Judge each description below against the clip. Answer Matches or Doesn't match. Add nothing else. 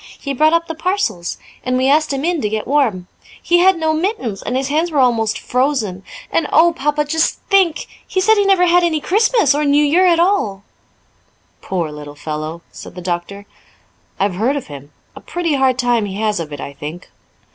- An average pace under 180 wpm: Doesn't match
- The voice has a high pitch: Matches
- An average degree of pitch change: Doesn't match